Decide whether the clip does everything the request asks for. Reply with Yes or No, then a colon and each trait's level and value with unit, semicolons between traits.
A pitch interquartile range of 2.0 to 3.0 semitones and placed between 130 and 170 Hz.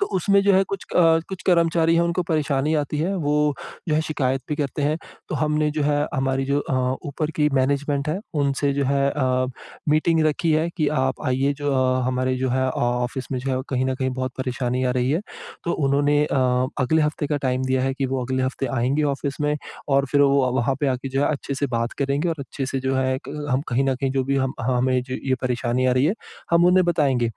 Yes: narrow, 2.5 semitones; medium, 140 Hz